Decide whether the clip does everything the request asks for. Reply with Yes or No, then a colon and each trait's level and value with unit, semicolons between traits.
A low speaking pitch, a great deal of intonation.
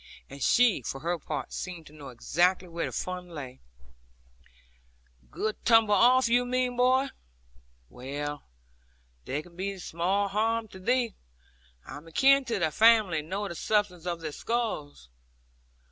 No: medium, 185 Hz; wide, 6.5 semitones